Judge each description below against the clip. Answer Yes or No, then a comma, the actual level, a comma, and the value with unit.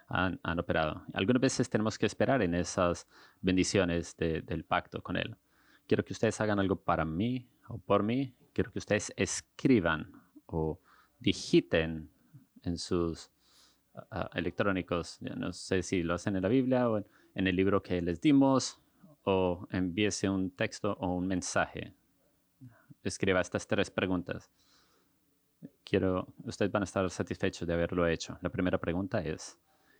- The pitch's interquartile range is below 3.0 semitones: No, average, 3.4 semitones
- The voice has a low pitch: Yes, very low, 95 Hz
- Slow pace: No, average, 150 wpm